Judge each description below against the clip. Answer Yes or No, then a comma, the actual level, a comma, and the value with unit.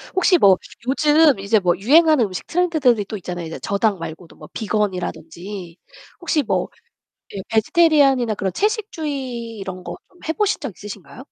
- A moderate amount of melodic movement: No, wide, 8.0 semitones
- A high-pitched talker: Yes, high, 220 Hz